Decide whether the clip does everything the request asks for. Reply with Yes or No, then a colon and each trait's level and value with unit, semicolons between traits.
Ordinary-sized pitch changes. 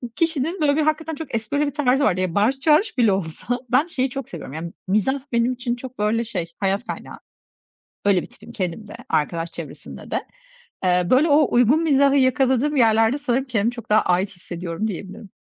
No: wide, 5.9 semitones